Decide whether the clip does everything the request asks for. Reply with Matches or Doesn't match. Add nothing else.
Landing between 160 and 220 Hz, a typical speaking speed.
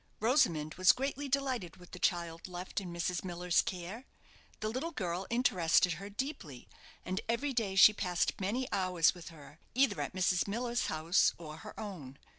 Matches